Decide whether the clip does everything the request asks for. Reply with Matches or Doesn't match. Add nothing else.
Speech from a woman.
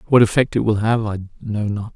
Doesn't match